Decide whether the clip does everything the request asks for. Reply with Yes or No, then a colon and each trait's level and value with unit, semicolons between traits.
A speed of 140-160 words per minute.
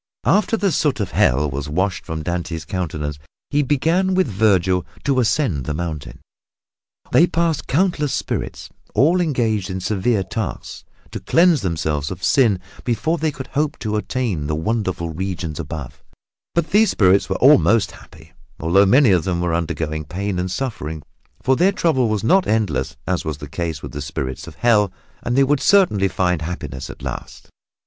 No: average, 170 wpm